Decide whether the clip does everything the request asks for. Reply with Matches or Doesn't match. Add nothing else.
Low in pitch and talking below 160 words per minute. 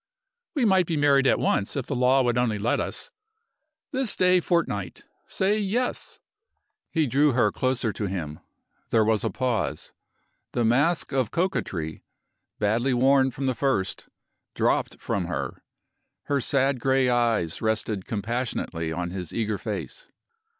Matches